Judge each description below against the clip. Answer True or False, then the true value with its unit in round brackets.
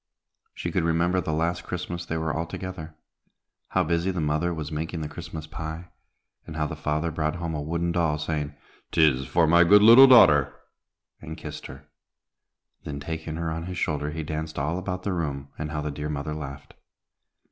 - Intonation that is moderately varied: False (2.1 semitones)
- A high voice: False (80 Hz)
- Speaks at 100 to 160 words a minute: False (190 wpm)